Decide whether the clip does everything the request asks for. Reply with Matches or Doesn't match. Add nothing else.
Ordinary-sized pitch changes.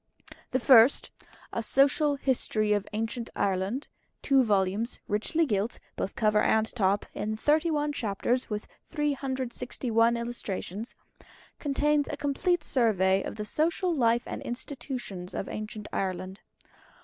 Matches